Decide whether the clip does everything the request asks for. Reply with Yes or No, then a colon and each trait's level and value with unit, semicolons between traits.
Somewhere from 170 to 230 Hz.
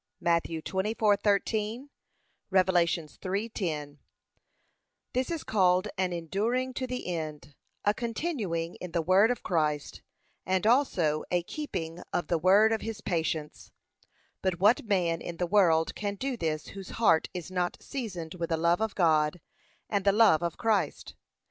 Yes: medium, 185 Hz